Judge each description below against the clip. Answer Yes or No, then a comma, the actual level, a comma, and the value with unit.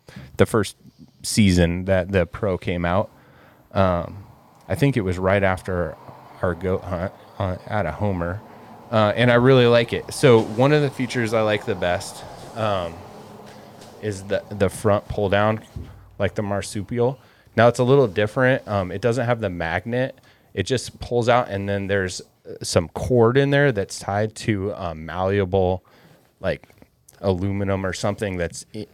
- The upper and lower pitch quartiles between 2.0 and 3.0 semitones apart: No, average, 3.7 semitones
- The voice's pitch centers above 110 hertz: No, low, 105 Hz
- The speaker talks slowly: No, average, 170 wpm